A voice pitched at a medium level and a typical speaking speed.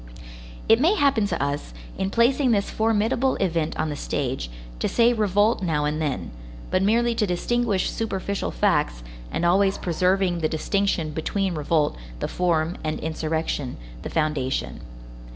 Yes: medium, 180 Hz; average, 150 wpm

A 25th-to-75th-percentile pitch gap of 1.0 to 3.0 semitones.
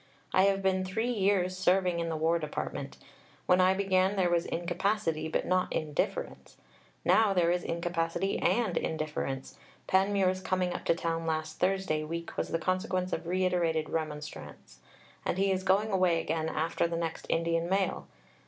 Yes: narrow, 2.4 semitones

